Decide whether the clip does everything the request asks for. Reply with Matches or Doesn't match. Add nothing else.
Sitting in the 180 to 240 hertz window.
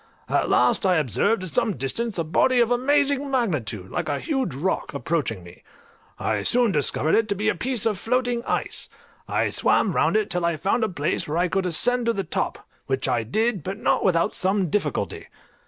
Matches